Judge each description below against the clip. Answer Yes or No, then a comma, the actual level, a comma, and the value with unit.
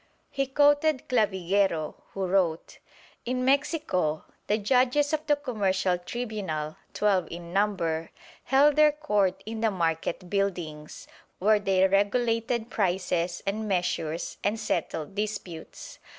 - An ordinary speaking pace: No, slow, 120 wpm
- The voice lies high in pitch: Yes, high, 200 Hz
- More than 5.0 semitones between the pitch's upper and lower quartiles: Yes, wide, 5.6 semitones